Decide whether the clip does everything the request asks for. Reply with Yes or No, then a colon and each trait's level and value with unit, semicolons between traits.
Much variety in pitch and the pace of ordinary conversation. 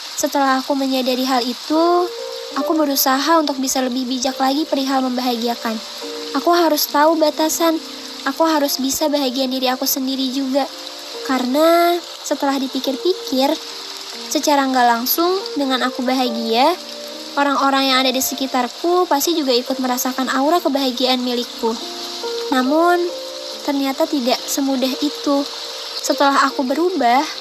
No: average, 3.2 semitones; average, 120 wpm